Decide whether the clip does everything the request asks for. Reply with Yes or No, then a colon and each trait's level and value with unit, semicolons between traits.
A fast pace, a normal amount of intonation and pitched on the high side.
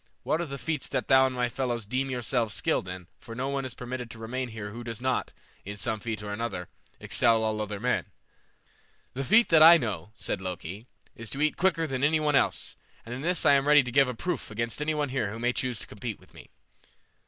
No: fast, 240 wpm; average, 3.8 semitones; low, 125 Hz